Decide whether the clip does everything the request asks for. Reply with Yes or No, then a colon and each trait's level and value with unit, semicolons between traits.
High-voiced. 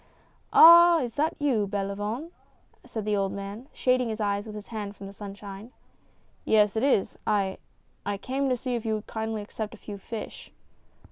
Yes: high, 215 Hz